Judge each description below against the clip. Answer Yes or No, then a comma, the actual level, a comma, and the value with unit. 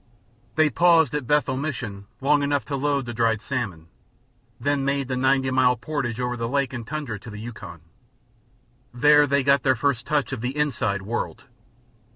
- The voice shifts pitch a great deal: No, average, 3.3 semitones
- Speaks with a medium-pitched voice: No, low, 130 Hz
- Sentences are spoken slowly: No, average, 175 wpm